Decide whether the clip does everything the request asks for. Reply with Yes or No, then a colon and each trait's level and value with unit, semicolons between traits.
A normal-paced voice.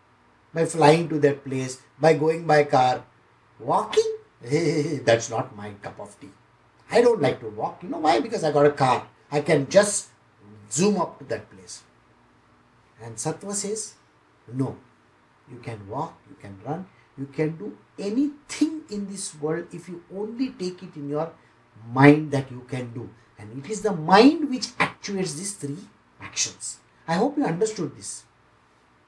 Yes: average, 165 wpm